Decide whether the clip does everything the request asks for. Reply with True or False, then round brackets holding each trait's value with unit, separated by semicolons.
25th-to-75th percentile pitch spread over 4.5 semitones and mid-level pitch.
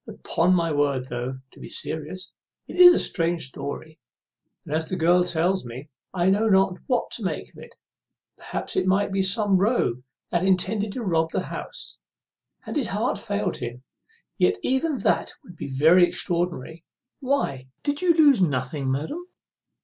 True (5.2 semitones; 180 Hz)